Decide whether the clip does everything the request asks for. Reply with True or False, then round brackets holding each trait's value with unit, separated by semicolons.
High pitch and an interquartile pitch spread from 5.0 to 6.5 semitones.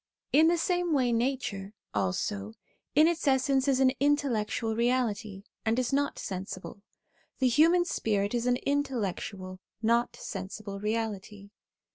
True (235 Hz; 5.3 semitones)